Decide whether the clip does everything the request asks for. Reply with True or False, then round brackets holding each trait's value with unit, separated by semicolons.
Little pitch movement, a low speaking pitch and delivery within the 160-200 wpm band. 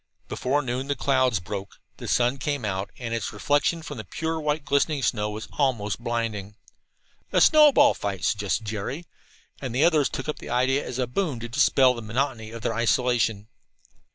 False (4.6 semitones; 125 Hz; 180 wpm)